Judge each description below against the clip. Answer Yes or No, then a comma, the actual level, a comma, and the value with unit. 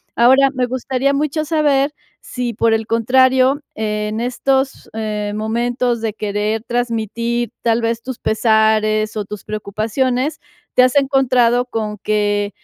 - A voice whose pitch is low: No, high, 235 Hz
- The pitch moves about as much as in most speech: Yes, average, 3.1 semitones